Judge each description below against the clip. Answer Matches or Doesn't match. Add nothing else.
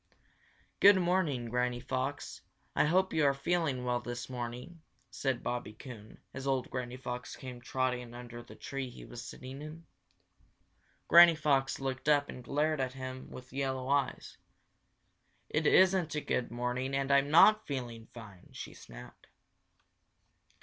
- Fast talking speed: Doesn't match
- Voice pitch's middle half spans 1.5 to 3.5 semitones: Matches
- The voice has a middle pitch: Doesn't match